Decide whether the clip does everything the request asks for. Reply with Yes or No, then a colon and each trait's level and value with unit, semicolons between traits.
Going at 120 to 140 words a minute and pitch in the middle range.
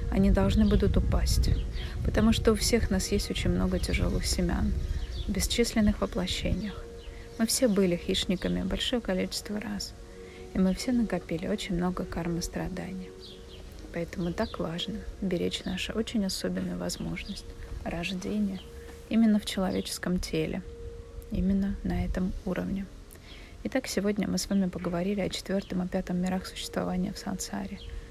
Yes: average, 135 wpm; medium, 175 Hz